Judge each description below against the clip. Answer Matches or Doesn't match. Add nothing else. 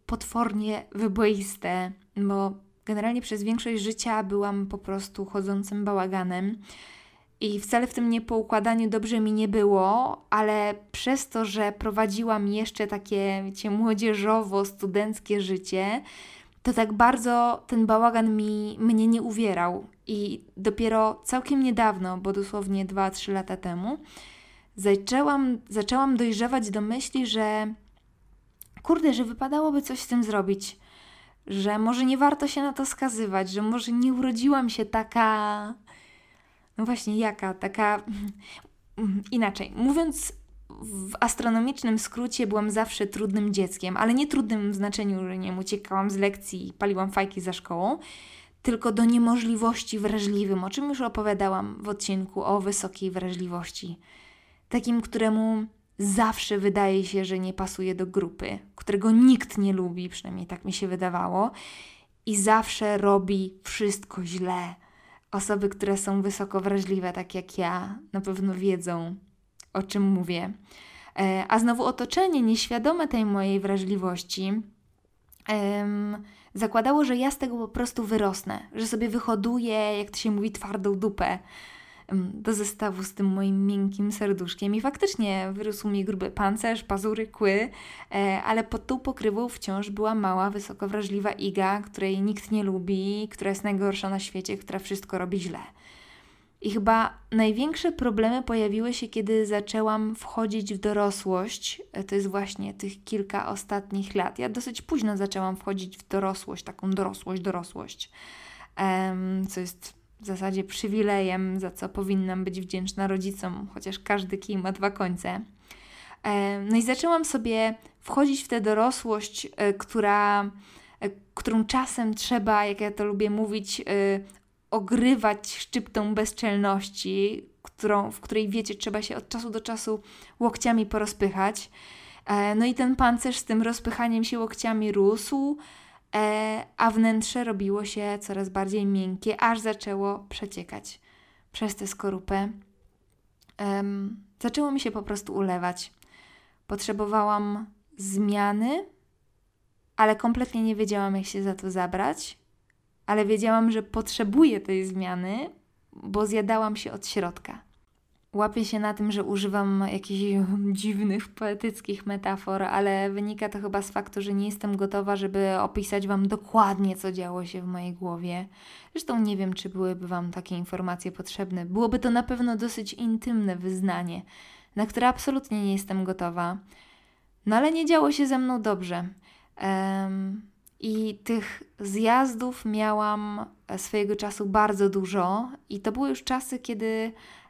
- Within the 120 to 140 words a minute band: Matches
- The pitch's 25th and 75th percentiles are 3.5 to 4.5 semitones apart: Doesn't match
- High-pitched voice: Matches